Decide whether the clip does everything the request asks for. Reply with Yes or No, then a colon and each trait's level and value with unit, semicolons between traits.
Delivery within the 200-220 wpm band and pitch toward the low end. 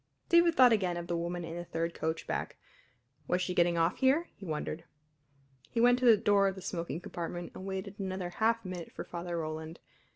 No: fast, 205 wpm; medium, 180 Hz